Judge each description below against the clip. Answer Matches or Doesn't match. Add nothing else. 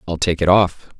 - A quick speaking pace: Matches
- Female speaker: Doesn't match